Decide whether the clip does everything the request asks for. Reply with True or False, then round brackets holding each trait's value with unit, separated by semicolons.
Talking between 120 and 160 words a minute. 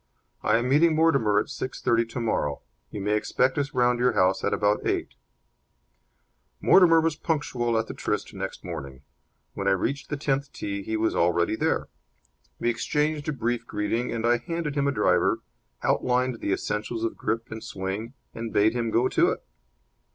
False (180 wpm)